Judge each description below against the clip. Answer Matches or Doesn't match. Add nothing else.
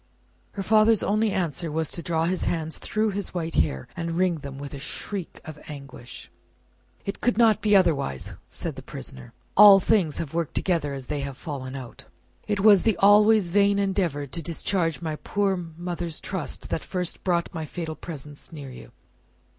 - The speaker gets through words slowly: Doesn't match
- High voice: Doesn't match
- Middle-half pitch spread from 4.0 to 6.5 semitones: Matches